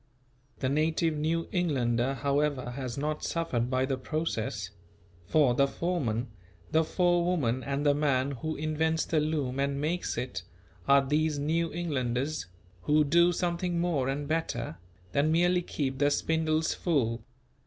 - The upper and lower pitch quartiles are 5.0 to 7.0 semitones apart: No, average, 3.7 semitones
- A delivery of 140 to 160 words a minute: Yes, average, 145 wpm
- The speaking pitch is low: No, medium, 150 Hz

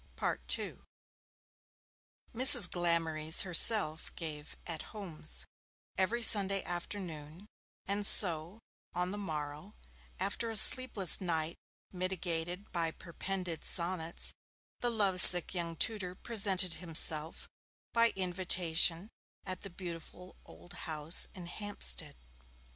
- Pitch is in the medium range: Yes, medium, 180 Hz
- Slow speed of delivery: Yes, slow, 105 wpm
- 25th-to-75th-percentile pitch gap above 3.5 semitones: No, average, 3.2 semitones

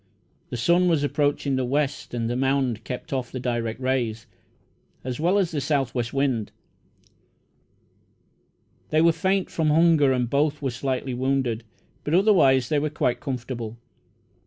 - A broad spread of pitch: No, average, 3.6 semitones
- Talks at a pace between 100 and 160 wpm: Yes, average, 155 wpm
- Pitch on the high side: No, low, 135 Hz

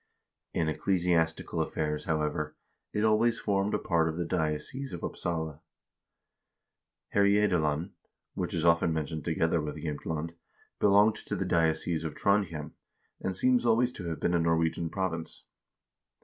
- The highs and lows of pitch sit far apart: No, average, 3.8 semitones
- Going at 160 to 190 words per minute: No, average, 140 wpm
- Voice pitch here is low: Yes, very low, 85 Hz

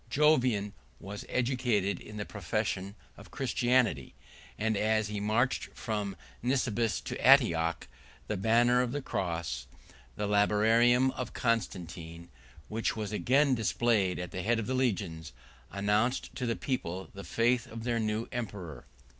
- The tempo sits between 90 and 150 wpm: Yes, average, 140 wpm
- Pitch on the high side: No, low, 110 Hz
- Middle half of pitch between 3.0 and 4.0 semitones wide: Yes, average, 3.6 semitones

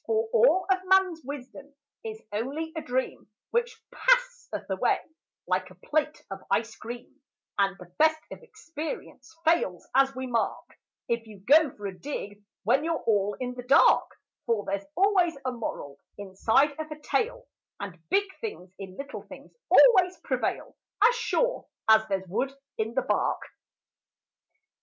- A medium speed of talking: Yes, average, 155 wpm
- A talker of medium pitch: No, very high, 270 Hz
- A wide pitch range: Yes, wide, 8.9 semitones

